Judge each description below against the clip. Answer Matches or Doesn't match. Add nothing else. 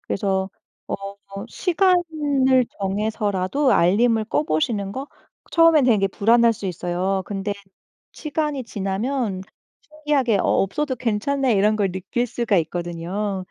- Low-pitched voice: Doesn't match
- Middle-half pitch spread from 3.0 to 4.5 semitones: Doesn't match